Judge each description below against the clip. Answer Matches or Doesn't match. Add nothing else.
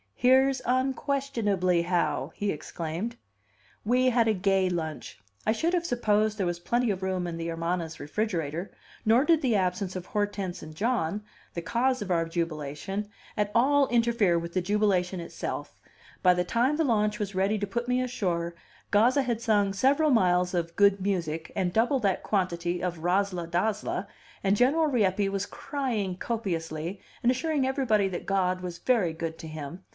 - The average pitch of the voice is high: Matches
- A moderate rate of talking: Matches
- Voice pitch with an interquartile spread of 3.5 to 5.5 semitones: Matches